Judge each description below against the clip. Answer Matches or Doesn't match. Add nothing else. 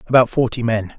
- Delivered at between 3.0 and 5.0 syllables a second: Doesn't match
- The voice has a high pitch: Doesn't match